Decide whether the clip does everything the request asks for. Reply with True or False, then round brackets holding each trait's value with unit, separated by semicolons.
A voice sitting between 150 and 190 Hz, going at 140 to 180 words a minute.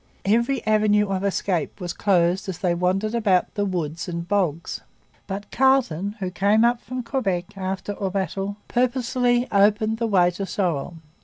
False (200 Hz; 175 wpm)